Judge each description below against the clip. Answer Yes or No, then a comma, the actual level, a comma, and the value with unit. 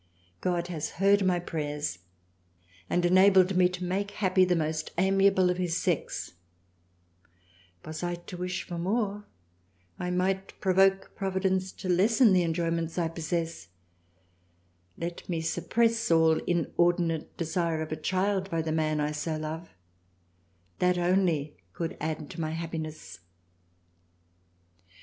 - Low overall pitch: No, medium, 175 Hz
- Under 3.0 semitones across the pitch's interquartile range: Yes, narrow, 2.6 semitones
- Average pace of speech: No, slow, 130 wpm